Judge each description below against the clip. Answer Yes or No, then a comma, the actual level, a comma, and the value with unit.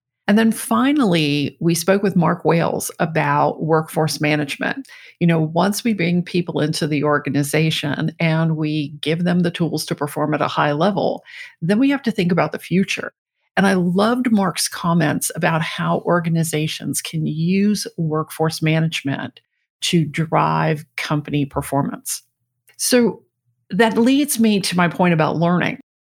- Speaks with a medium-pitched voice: Yes, medium, 165 Hz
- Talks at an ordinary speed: Yes, average, 150 wpm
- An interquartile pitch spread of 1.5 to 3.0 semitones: No, average, 4.1 semitones